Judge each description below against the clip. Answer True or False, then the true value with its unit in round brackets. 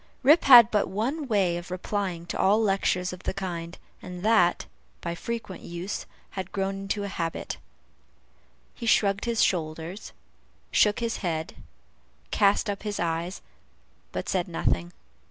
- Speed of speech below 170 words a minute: True (145 wpm)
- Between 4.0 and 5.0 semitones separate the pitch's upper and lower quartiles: False (3.4 semitones)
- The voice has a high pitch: True (195 Hz)